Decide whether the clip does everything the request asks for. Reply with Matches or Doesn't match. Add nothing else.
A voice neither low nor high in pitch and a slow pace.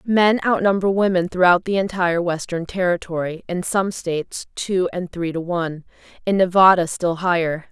Doesn't match